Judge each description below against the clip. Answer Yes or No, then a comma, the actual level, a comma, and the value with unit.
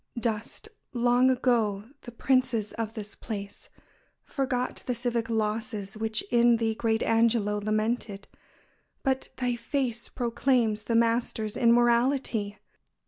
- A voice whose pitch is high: Yes, high, 230 Hz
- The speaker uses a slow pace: Yes, slow, 115 wpm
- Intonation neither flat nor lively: No, narrow, 2.2 semitones